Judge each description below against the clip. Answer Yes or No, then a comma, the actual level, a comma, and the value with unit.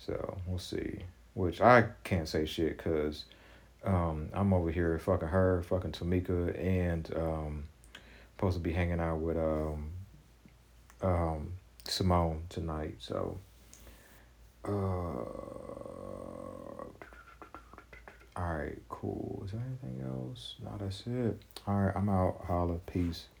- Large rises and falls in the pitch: No, average, 3.7 semitones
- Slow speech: Yes, slow, 125 wpm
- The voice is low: Yes, very low, 90 Hz